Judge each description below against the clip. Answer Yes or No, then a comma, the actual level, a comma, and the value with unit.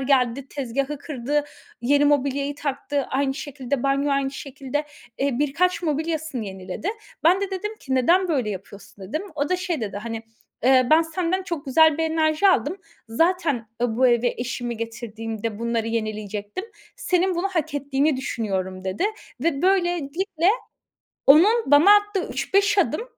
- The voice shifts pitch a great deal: Yes, wide, 5.8 semitones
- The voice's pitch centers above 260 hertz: Yes, very high, 280 Hz